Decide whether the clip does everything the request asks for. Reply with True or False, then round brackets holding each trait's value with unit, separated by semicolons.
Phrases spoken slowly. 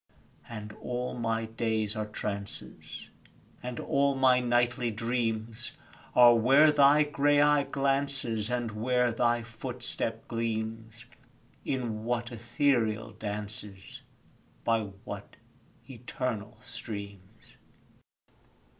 True (95 wpm)